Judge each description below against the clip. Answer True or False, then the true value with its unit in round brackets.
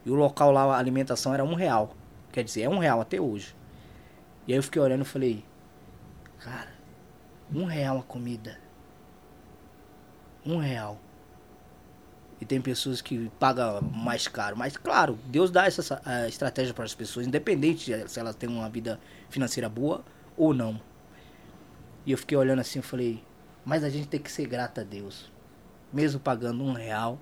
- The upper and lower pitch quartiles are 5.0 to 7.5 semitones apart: False (3.9 semitones)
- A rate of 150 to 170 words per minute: True (165 wpm)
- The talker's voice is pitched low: True (130 Hz)